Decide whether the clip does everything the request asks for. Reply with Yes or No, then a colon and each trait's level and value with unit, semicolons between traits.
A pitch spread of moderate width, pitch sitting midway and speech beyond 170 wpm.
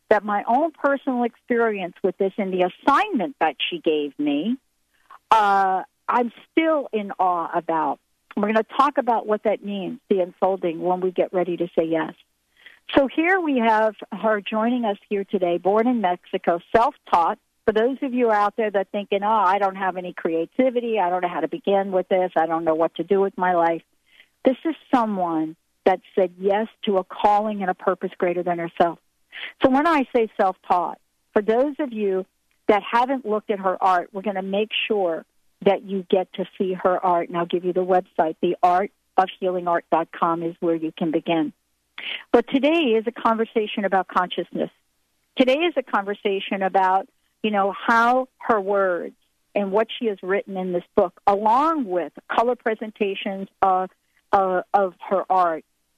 No: average, 4.0 semitones; high, 195 Hz; average, 180 wpm